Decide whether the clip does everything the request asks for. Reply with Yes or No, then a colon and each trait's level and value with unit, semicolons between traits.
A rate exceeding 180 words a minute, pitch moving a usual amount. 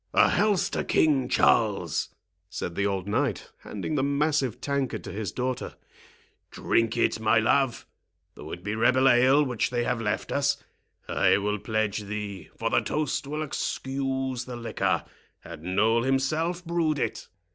No: average, 155 wpm; average, 4.8 semitones